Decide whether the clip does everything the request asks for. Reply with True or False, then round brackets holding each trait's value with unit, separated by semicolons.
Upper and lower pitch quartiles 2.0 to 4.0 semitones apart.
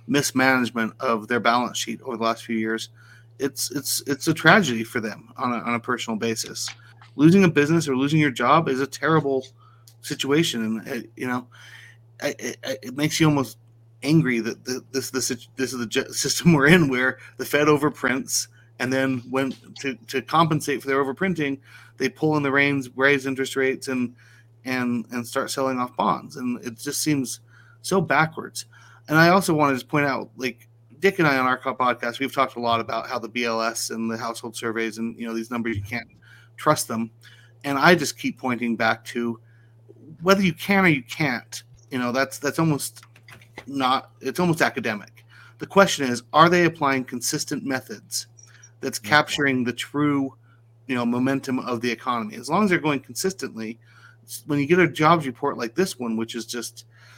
True (3.6 semitones)